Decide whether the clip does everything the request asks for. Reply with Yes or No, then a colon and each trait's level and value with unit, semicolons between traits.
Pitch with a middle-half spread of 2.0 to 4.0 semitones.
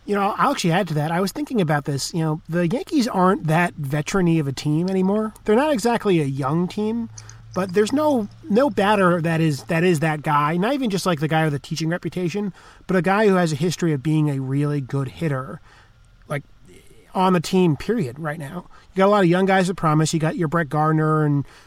No: average, 4.4 semitones